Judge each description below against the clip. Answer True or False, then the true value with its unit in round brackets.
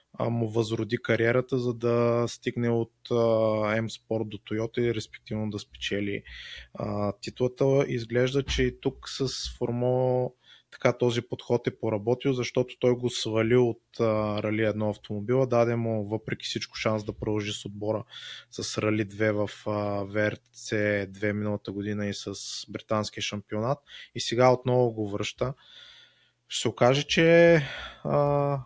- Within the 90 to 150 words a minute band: True (135 wpm)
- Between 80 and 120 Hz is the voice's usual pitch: True (115 Hz)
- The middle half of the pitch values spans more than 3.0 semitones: False (2.7 semitones)